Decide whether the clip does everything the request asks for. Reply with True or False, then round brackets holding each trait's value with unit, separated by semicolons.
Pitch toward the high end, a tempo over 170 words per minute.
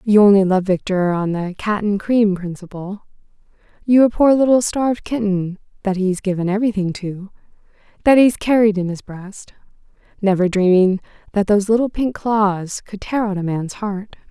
False (200 Hz; 165 wpm)